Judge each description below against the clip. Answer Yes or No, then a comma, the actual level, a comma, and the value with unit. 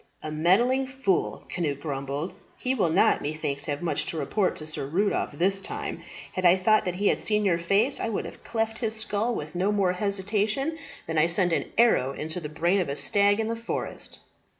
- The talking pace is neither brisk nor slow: No, fast, 210 wpm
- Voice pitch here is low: No, medium, 185 Hz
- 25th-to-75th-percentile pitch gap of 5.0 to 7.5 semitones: Yes, wide, 5.4 semitones